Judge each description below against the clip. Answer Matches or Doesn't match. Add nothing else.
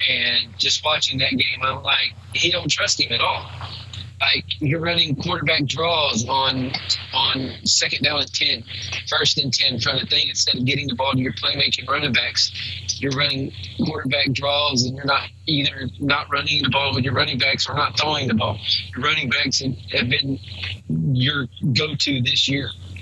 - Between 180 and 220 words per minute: Matches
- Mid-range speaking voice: Doesn't match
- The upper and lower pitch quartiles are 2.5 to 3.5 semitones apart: Doesn't match